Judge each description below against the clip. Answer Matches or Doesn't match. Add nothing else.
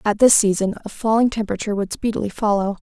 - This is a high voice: Matches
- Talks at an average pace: Matches